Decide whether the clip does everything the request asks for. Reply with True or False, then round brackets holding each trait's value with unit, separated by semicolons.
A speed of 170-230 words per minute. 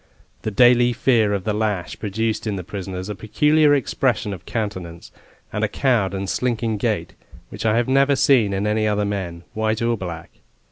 True (185 wpm)